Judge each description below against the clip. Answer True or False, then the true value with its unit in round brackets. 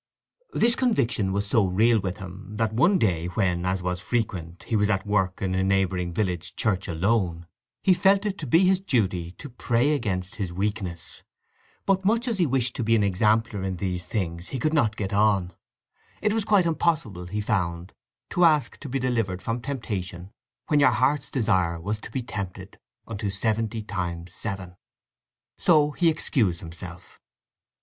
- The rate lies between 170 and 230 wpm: True (175 wpm)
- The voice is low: True (105 Hz)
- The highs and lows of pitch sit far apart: True (5.9 semitones)